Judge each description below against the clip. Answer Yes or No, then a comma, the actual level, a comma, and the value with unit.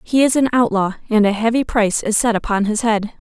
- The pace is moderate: No, fast, 240 wpm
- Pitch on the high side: Yes, high, 220 Hz